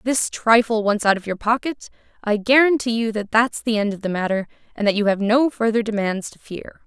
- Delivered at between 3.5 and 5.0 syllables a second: No, 5.4 syllables/s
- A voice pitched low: No, high, 220 Hz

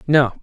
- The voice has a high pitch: No, low, 135 Hz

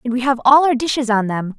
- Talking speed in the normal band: No, fast, 305 wpm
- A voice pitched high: Yes, very high, 250 Hz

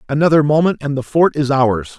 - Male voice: Yes, male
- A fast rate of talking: Yes, fast, 210 wpm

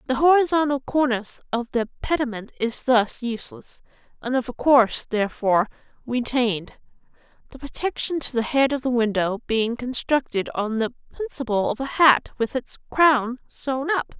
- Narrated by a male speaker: No, female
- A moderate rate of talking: Yes, average, 150 wpm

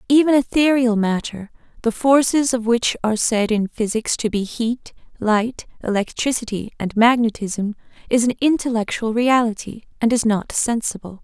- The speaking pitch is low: No, high, 230 Hz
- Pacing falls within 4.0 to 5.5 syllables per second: Yes, 4.8 syllables/s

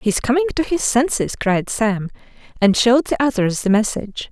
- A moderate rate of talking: Yes, average, 180 wpm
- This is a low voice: No, high, 240 Hz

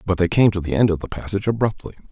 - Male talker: Yes, male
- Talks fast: Yes, fast, 285 wpm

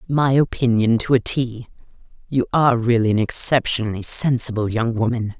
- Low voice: Yes, low, 120 Hz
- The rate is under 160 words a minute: Yes, average, 145 wpm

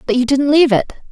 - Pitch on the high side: Yes, very high, 265 Hz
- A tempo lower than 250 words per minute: No, fast, 270 wpm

